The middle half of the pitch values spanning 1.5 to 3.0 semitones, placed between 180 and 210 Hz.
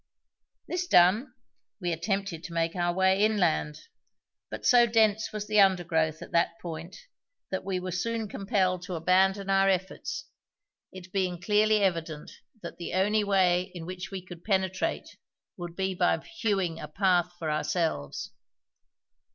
Yes: narrow, 2.6 semitones; medium, 185 Hz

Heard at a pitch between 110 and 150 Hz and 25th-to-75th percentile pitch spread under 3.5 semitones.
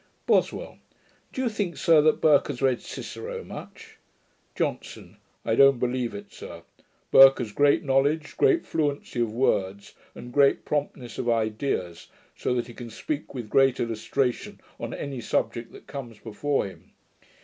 No: low, 135 Hz; average, 3.8 semitones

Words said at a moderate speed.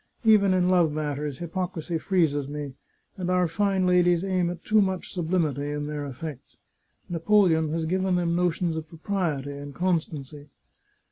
Yes: average, 150 wpm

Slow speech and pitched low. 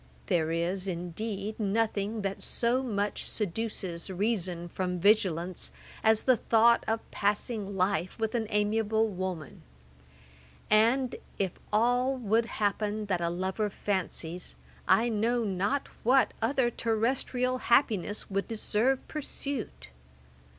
No: slow, 115 wpm; high, 210 Hz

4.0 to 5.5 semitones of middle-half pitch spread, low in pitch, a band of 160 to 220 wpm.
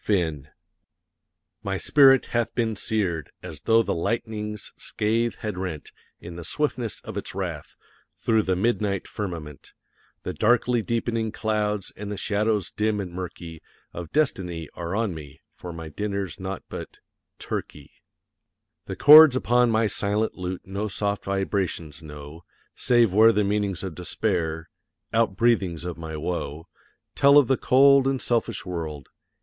No: average, 4.7 semitones; low, 100 Hz; average, 145 wpm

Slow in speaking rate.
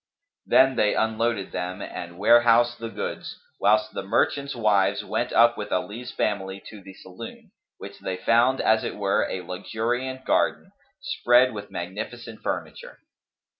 No: average, 145 wpm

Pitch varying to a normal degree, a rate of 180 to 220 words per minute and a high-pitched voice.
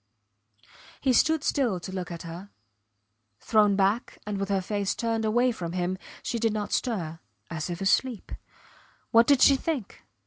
No: average, 4.3 semitones; average, 165 wpm; high, 210 Hz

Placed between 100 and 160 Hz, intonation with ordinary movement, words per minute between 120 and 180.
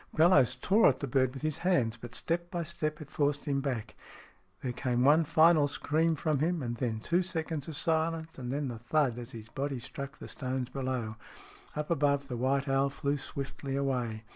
No: medium, 140 Hz; average, 3.7 semitones; average, 200 wpm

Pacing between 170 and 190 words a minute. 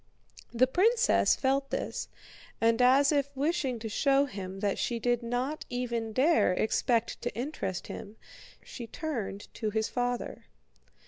No: average, 140 wpm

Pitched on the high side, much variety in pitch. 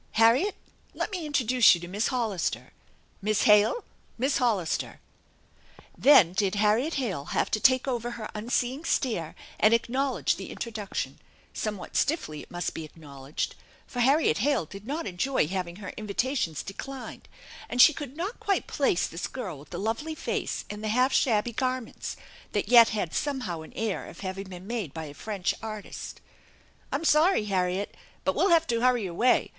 Yes: high, 220 Hz; wide, 5.7 semitones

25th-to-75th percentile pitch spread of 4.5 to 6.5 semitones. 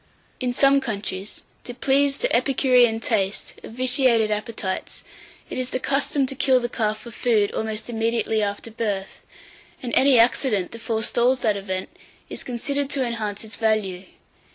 No: average, 3.2 semitones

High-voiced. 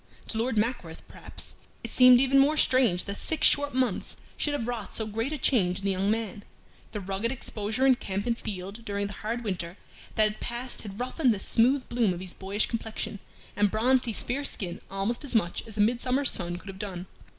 Yes: high, 220 Hz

